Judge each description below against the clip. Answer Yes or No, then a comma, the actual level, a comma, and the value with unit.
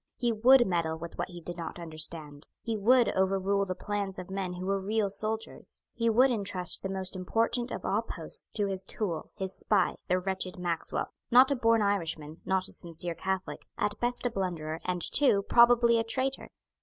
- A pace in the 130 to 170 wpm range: No, average, 195 wpm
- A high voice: Yes, high, 195 Hz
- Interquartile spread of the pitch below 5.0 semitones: Yes, average, 4.1 semitones